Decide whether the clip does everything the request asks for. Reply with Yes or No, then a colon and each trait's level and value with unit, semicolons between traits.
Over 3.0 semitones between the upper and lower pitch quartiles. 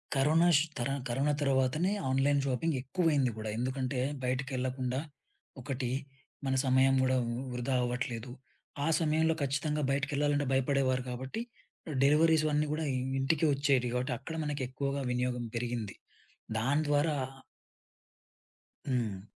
No: narrow, 2.6 semitones